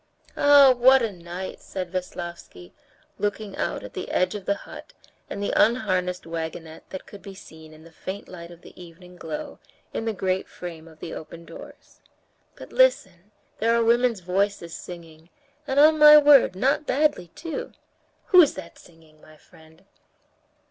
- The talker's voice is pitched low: No, medium, 185 Hz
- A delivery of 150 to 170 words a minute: Yes, average, 165 wpm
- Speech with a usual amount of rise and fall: No, wide, 5.7 semitones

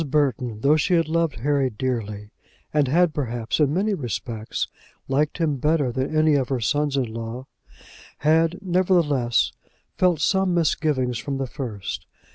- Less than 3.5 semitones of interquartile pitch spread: No, average, 4.4 semitones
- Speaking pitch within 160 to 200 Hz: No, medium, 140 Hz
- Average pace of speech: Yes, average, 150 wpm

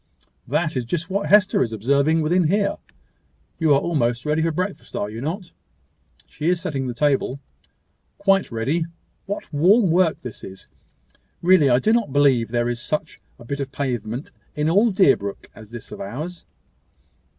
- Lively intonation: Yes, wide, 6.5 semitones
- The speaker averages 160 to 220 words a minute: Yes, average, 170 wpm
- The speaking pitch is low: No, medium, 150 Hz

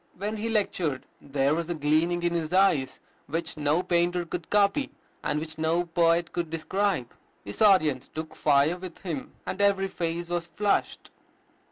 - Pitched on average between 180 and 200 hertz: No, medium, 170 Hz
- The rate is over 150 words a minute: Yes, average, 165 wpm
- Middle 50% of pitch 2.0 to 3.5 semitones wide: Yes, average, 2.9 semitones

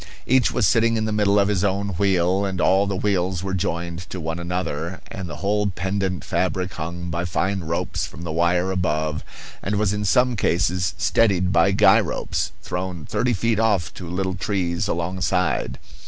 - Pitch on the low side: Yes, very low, 95 Hz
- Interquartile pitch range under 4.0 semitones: Yes, narrow, 2.6 semitones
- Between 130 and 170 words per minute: No, average, 185 wpm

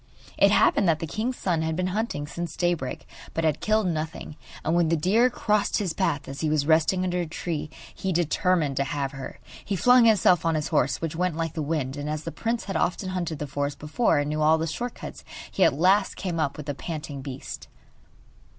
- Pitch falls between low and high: Yes, medium, 165 Hz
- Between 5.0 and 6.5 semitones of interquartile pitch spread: No, average, 3.7 semitones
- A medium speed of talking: No, fast, 225 wpm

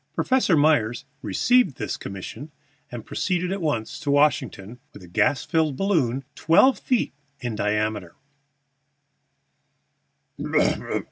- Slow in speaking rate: Yes, slow, 105 wpm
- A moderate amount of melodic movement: No, wide, 7.4 semitones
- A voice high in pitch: No, low, 135 Hz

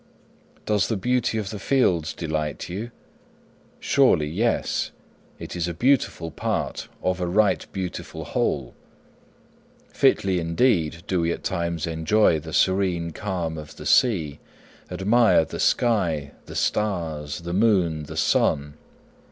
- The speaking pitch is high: No, very low, 90 Hz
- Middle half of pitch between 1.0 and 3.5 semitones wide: No, average, 4.6 semitones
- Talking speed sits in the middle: No, slow, 130 wpm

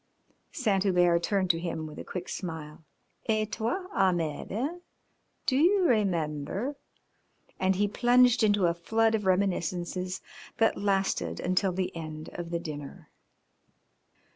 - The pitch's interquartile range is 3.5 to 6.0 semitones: Yes, average, 4.4 semitones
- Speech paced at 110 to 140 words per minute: Yes, slow, 135 wpm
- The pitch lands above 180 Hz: Yes, high, 190 Hz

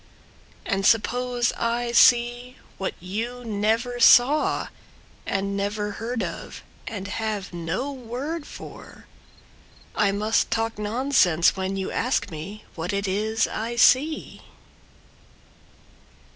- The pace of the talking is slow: Yes, slow, 110 wpm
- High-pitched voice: Yes, high, 225 Hz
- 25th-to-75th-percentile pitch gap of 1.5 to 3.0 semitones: No, average, 3.5 semitones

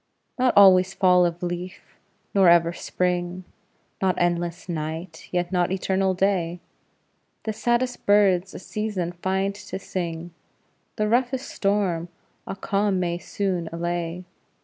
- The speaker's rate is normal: No, slow, 125 wpm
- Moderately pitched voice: Yes, medium, 180 Hz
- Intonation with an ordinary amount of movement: No, narrow, 2.2 semitones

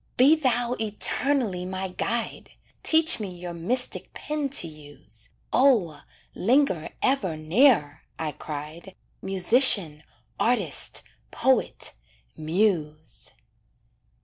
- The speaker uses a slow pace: Yes, slow, 95 wpm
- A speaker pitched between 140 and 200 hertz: Yes, high, 190 Hz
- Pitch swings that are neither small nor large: No, wide, 8.1 semitones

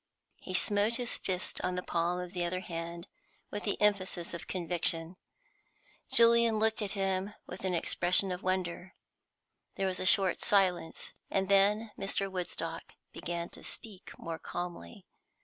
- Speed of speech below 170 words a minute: Yes, average, 150 wpm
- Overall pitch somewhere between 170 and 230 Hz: Yes, medium, 185 Hz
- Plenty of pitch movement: No, narrow, 2.4 semitones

